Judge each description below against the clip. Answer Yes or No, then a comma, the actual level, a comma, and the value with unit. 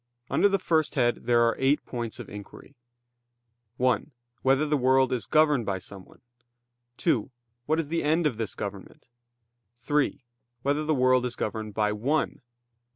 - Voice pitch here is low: Yes, low, 130 Hz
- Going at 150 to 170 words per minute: Yes, average, 155 wpm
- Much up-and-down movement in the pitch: No, average, 5.0 semitones